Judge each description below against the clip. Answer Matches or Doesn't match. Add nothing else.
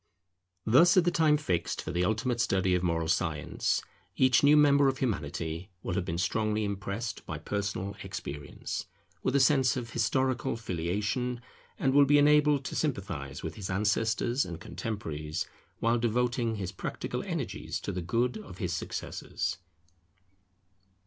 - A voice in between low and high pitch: Doesn't match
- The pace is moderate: Matches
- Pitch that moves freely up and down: Matches